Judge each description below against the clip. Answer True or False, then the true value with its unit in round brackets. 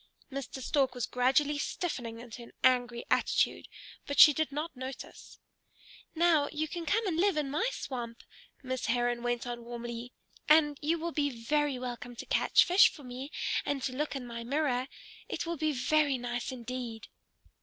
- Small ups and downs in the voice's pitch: False (3.7 semitones)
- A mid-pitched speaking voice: False (260 Hz)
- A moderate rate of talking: True (175 wpm)